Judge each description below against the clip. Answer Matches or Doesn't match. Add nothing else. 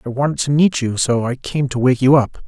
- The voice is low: Matches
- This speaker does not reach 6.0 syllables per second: Matches